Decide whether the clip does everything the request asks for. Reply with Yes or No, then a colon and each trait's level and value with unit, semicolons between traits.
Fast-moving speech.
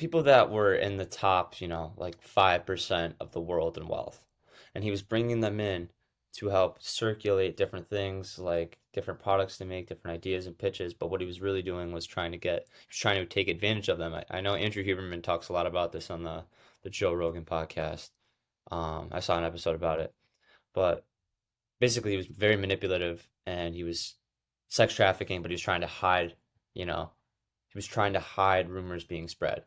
Yes: fast, 210 wpm